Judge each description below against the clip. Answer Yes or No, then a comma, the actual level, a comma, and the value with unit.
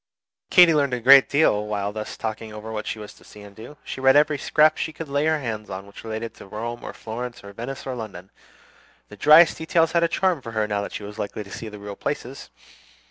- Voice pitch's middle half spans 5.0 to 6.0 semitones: Yes, wide, 5.5 semitones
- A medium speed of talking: No, fast, 245 wpm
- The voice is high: No, low, 115 Hz